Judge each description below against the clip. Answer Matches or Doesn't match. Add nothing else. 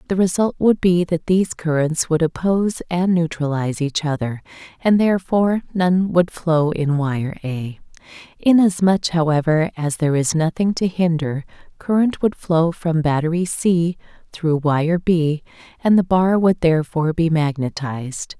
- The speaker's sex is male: Doesn't match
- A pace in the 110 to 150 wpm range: Matches